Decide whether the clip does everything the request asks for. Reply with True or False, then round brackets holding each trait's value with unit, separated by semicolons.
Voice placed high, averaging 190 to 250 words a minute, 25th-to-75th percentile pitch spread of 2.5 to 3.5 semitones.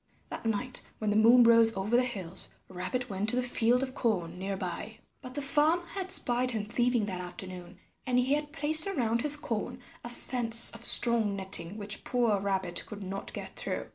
False (230 Hz; 200 wpm; 4.2 semitones)